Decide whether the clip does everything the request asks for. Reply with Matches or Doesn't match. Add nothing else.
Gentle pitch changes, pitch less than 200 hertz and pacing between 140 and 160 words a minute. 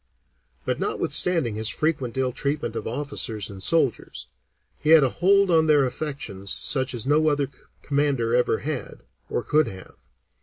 Doesn't match